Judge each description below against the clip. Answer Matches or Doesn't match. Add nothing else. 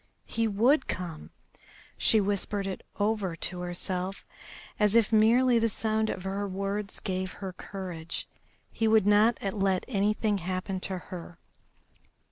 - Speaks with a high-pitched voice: Matches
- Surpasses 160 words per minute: Doesn't match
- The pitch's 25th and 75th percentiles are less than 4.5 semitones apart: Matches